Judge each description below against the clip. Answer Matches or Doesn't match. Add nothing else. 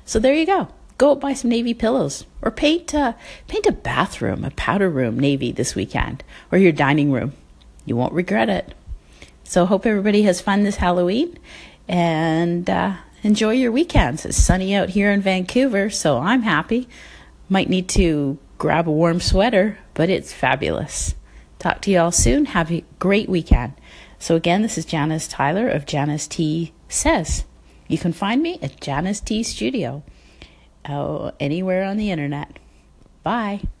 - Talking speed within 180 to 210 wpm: Doesn't match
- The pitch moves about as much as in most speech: Doesn't match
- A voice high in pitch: Doesn't match